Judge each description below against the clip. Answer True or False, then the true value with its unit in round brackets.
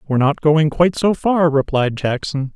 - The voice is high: False (150 Hz)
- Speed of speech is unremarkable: True (190 wpm)